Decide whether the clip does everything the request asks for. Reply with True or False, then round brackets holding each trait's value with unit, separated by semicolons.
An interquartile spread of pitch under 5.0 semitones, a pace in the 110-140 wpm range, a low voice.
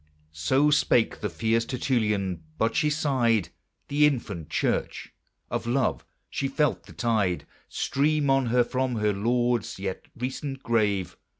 True (4.2 semitones; 135 wpm; 120 Hz)